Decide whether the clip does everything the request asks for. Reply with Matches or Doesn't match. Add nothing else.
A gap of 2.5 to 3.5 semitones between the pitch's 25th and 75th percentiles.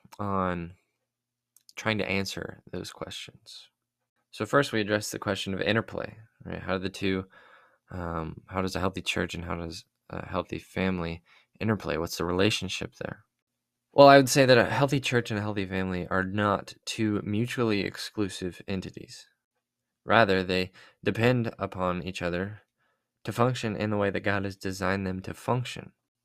Matches